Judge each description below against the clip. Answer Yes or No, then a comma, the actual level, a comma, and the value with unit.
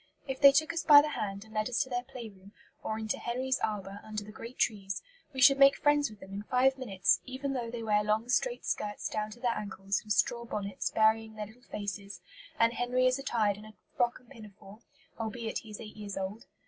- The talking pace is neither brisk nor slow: No, fast, 225 wpm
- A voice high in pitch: Yes, high, 220 Hz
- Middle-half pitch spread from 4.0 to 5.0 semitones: No, average, 3.4 semitones